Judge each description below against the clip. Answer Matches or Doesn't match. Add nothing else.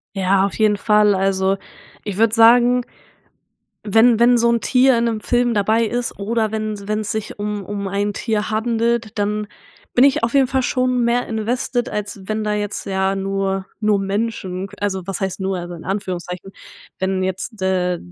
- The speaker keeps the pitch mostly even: Doesn't match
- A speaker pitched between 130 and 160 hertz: Doesn't match